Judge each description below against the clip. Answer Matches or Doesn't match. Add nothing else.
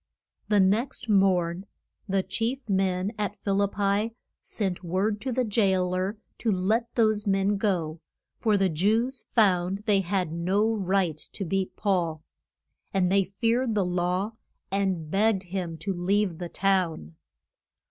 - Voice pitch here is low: Doesn't match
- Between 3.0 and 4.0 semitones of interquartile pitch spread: Doesn't match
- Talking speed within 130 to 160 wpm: Matches